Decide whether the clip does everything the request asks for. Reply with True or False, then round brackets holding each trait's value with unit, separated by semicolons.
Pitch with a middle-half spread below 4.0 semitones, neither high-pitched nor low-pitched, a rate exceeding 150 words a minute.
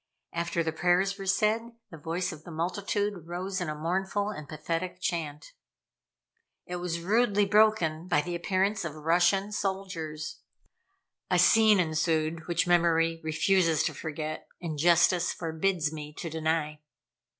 False (3.3 semitones; 170 Hz; 145 wpm)